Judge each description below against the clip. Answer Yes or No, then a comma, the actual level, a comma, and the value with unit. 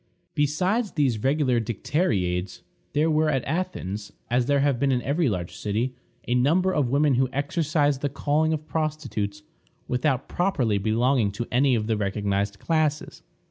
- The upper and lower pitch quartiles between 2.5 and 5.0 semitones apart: No, wide, 5.6 semitones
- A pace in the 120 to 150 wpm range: No, average, 160 wpm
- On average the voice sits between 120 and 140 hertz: Yes, low, 135 Hz